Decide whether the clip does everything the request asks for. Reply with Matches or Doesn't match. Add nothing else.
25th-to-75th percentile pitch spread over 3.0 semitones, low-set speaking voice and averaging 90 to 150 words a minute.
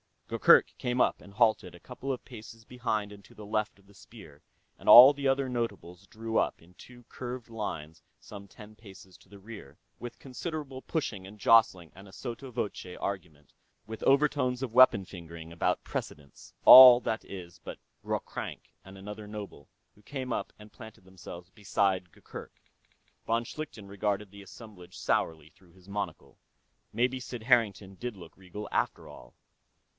Doesn't match